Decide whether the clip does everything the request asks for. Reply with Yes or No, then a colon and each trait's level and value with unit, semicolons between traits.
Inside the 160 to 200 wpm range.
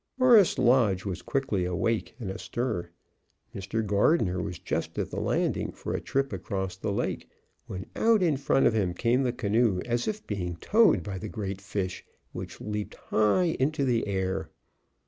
Yes: average, 170 wpm